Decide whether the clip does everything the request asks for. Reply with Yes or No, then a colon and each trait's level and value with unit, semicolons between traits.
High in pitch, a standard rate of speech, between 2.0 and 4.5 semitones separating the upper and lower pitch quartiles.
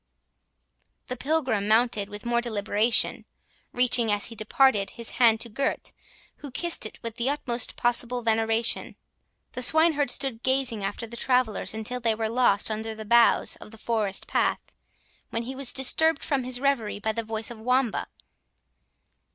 Yes: high, 235 Hz; average, 160 wpm; narrow, 2.6 semitones